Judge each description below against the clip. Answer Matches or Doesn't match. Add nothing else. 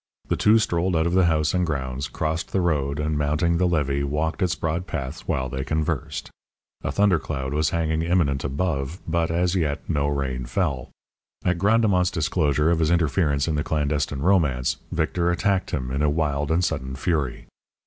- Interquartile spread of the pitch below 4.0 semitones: Matches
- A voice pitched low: Matches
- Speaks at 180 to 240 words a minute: Matches